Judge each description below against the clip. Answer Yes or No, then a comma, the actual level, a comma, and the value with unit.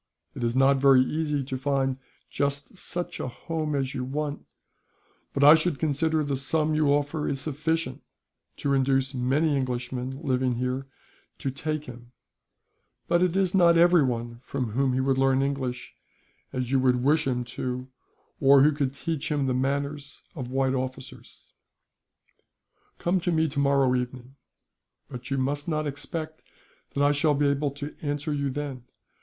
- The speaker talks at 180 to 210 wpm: No, average, 165 wpm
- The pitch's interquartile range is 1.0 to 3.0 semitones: Yes, narrow, 2.5 semitones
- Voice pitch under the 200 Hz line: Yes, medium, 140 Hz